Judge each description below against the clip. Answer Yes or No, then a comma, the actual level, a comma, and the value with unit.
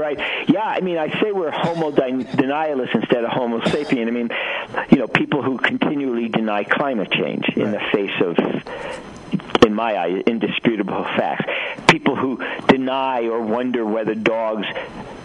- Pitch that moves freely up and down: No, average, 3.3 semitones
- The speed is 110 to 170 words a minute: Yes, average, 155 wpm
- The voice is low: Yes, low, 120 Hz